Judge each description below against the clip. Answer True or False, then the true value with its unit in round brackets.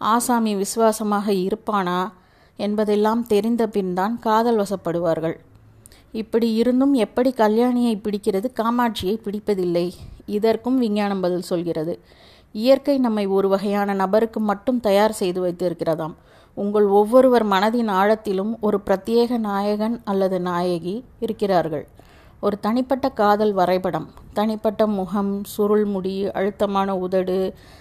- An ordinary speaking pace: True (105 wpm)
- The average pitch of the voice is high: True (205 Hz)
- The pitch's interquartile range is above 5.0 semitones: False (2.9 semitones)